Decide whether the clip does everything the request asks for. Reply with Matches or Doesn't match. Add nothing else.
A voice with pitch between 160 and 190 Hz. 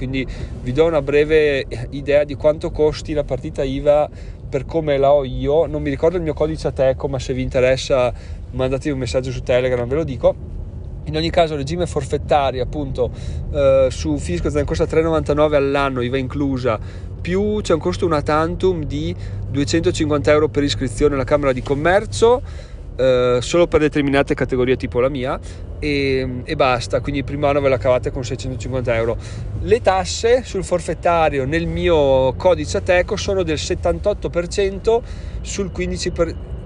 Doesn't match